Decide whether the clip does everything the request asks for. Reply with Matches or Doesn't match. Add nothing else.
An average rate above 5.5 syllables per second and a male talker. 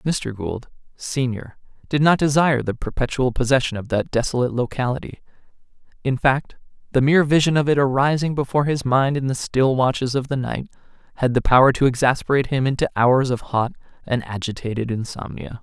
Matches